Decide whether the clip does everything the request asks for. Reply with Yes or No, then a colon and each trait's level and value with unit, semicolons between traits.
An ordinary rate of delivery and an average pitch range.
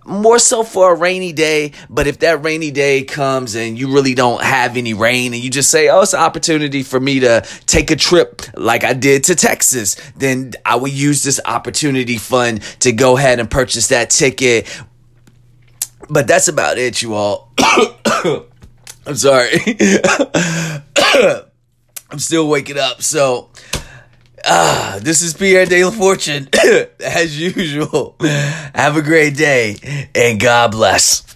Yes: average, 155 wpm; average, 4.7 semitones